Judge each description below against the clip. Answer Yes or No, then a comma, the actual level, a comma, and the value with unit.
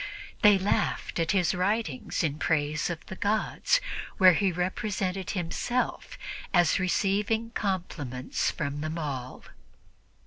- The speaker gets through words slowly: Yes, slow, 115 wpm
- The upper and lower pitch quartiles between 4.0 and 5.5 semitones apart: Yes, average, 4.4 semitones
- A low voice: No, medium, 180 Hz